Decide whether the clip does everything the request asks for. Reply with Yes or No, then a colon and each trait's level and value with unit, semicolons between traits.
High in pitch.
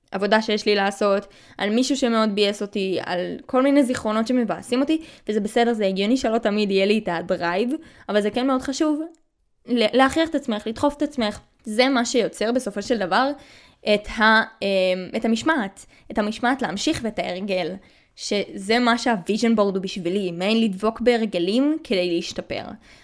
Yes: high, 220 Hz